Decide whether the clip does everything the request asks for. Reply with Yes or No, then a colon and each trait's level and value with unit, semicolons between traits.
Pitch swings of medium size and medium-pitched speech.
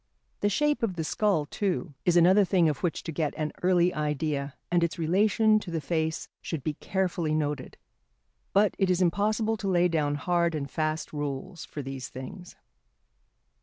Yes: average, 3.8 semitones; medium, 170 Hz